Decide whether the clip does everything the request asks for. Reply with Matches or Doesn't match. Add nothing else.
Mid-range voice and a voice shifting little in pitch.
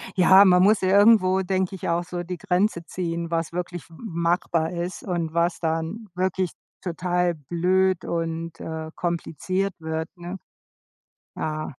Matches